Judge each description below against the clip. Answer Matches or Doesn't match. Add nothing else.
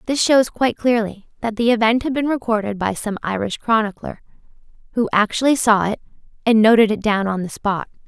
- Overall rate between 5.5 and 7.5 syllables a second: Matches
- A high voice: Matches